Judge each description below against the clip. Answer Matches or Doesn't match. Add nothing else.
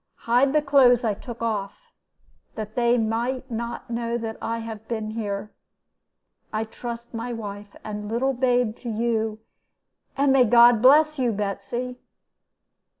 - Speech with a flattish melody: Matches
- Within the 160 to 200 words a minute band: Doesn't match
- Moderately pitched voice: Doesn't match